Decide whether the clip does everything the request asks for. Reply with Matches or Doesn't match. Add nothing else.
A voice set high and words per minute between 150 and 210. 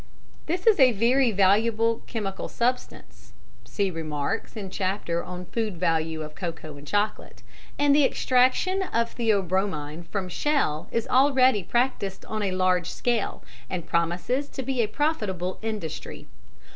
Doesn't match